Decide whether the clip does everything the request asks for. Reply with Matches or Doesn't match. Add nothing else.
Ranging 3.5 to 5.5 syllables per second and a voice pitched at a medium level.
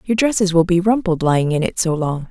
Doesn't match